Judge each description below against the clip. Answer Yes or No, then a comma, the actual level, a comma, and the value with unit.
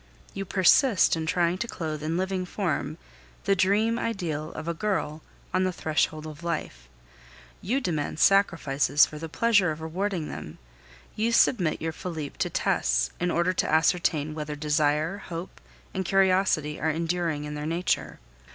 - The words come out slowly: No, average, 160 wpm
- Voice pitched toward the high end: No, medium, 165 Hz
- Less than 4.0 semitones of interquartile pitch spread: Yes, average, 3.6 semitones